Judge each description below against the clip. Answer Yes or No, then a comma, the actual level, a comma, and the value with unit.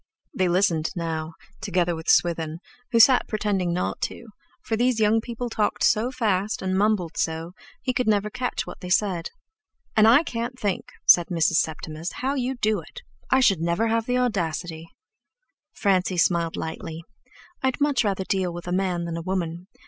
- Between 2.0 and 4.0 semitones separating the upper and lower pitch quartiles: No, average, 4.8 semitones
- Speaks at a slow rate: No, average, 175 wpm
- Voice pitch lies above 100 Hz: Yes, high, 190 Hz